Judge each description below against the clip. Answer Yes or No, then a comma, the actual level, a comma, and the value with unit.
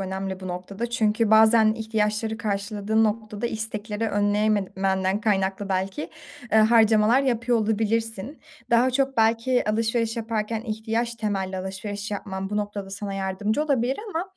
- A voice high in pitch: Yes, high, 215 Hz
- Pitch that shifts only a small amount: Yes, narrow, 2.2 semitones